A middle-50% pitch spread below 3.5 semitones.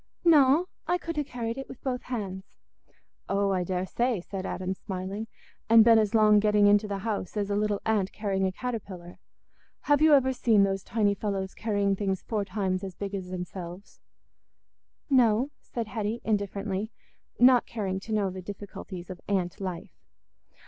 Yes: average, 3.1 semitones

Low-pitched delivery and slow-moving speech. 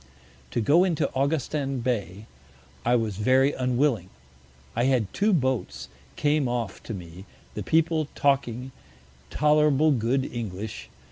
Yes: low, 130 Hz; slow, 125 wpm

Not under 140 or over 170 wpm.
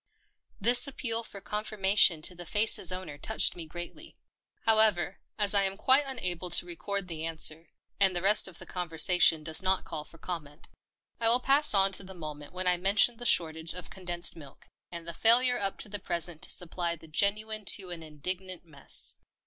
No: average, 195 wpm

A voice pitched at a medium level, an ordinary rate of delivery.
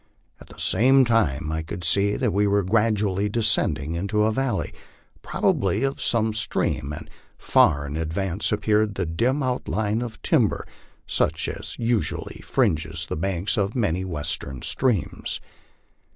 No: low, 100 Hz; average, 155 wpm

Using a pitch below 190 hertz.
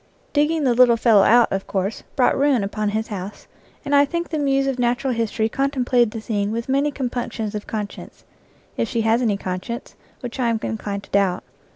No: high, 235 Hz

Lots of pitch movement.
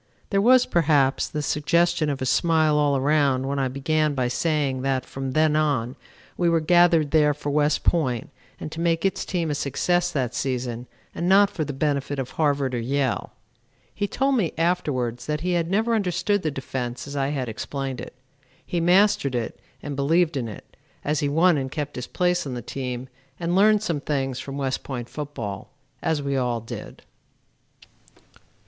No: average, 4.0 semitones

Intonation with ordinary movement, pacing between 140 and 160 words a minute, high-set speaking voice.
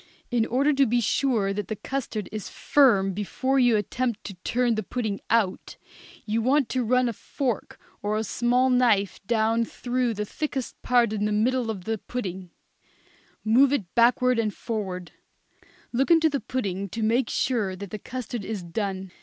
No: average, 3.5 semitones; average, 175 wpm; high, 230 Hz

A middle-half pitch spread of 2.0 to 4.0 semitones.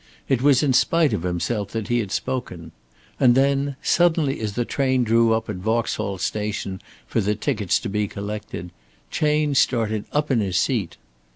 No: average, 4.9 semitones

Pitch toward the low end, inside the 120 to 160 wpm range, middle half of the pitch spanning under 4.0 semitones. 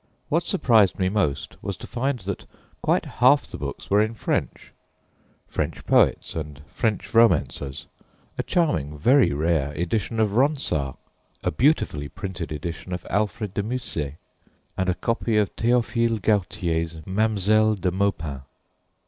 No: low, 100 Hz; average, 140 wpm; wide, 5.6 semitones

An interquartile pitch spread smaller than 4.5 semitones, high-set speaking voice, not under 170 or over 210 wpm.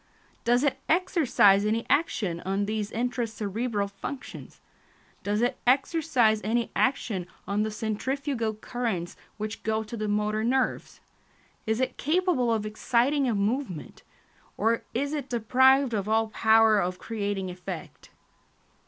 No: average, 3.5 semitones; high, 225 Hz; slow, 135 wpm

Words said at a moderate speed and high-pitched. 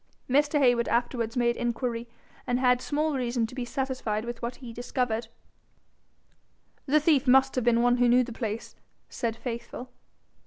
Yes: average, 160 wpm; high, 245 Hz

